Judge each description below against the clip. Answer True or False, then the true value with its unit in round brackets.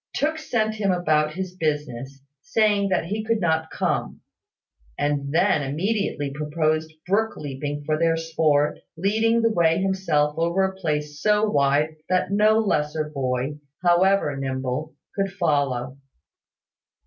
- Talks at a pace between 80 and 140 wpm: True (135 wpm)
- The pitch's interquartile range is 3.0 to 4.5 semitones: False (4.9 semitones)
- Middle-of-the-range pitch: True (160 Hz)